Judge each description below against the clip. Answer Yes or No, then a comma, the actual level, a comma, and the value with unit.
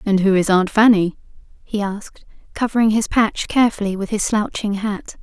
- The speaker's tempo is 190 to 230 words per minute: No, average, 170 wpm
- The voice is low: No, high, 210 Hz